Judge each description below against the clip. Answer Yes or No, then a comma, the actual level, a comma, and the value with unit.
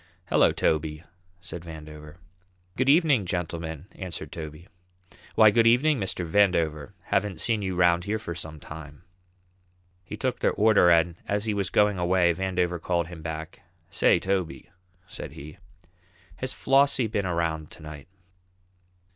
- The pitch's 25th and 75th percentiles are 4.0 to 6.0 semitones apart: Yes, average, 4.3 semitones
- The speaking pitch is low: Yes, very low, 90 Hz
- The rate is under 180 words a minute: Yes, average, 145 wpm